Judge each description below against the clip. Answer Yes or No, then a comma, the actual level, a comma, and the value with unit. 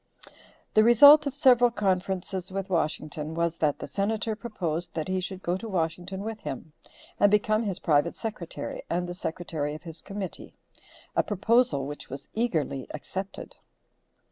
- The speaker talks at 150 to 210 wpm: Yes, average, 155 wpm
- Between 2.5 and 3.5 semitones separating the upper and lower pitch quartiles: No, average, 5.0 semitones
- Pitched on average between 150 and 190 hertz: Yes, medium, 185 Hz